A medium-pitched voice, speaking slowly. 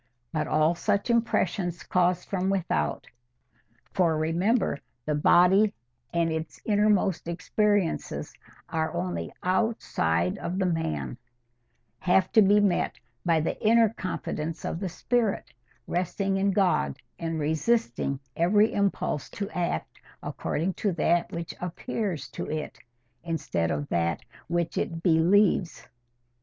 Yes: medium, 170 Hz; slow, 120 wpm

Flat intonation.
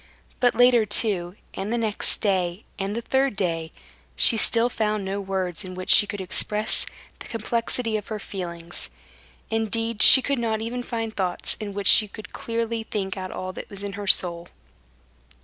No: average, 3.2 semitones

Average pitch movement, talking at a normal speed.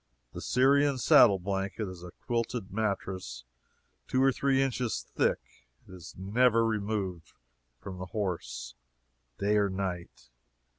No: average, 4.2 semitones; slow, 130 wpm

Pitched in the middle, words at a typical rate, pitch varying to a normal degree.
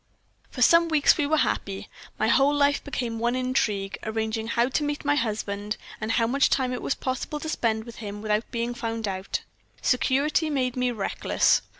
No: high, 245 Hz; average, 190 wpm; average, 4.4 semitones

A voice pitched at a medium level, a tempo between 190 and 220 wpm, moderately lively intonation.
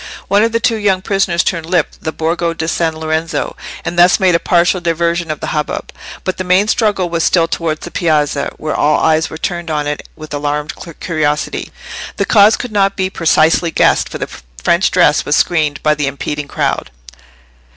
Yes: medium, 165 Hz; average, 195 wpm; average, 3.0 semitones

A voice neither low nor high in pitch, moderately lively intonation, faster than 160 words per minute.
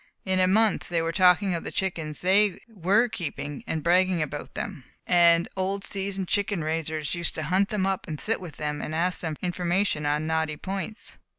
Yes: medium, 180 Hz; average, 3.3 semitones; average, 195 wpm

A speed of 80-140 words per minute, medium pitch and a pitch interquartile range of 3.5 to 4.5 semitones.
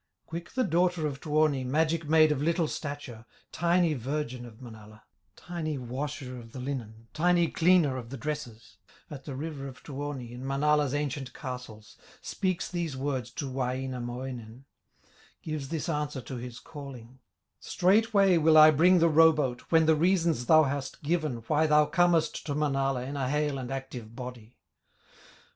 No: average, 160 wpm; medium, 145 Hz; average, 3.9 semitones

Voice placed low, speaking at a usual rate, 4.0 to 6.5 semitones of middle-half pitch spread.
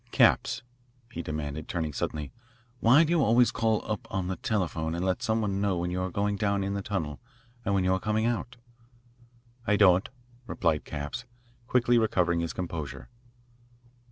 Yes: very low, 95 Hz; average, 175 wpm; average, 4.6 semitones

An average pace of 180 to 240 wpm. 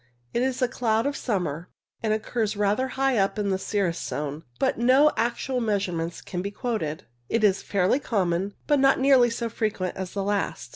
Yes: average, 190 wpm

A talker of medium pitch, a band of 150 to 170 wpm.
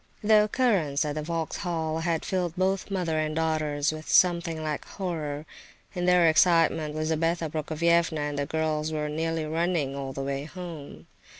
Yes: medium, 160 Hz; average, 160 wpm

